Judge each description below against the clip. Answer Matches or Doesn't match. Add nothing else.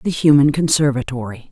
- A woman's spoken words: Matches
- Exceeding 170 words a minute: Doesn't match